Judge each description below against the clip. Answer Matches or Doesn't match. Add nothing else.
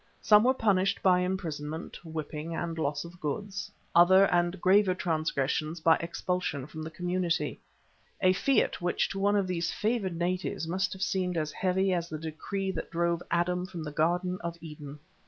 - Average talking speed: Matches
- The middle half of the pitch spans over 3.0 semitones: Doesn't match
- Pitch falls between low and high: Matches